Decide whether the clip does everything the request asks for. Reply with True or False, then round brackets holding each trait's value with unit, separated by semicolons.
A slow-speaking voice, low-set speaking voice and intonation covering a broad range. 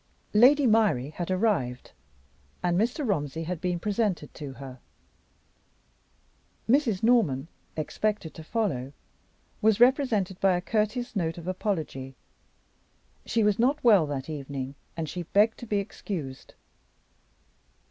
False (125 wpm; 185 Hz; 6.5 semitones)